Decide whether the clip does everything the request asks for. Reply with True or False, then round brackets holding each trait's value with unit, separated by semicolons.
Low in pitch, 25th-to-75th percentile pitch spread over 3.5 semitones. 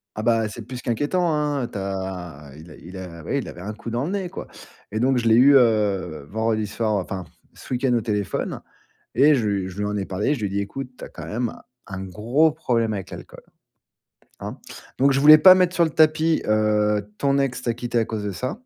True (115 Hz; 5.4 semitones)